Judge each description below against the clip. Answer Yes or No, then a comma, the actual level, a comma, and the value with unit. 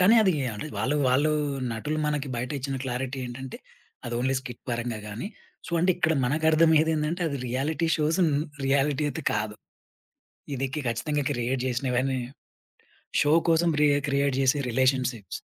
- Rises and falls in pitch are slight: No, average, 3.5 semitones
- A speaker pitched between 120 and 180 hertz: Yes, low, 135 Hz